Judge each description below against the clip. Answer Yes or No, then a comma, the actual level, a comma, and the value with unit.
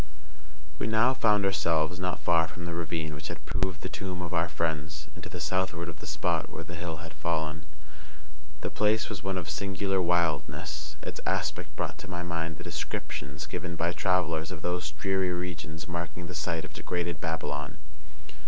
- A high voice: No, very low, 85 Hz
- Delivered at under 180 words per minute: No, average, 190 wpm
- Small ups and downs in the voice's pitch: Yes, narrow, 2.2 semitones